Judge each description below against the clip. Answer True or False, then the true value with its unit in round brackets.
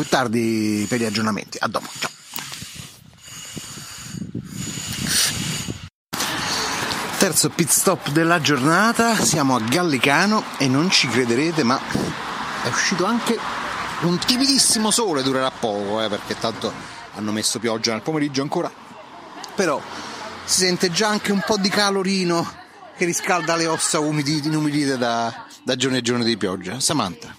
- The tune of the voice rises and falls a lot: True (7.5 semitones)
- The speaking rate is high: False (135 wpm)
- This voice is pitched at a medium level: True (150 Hz)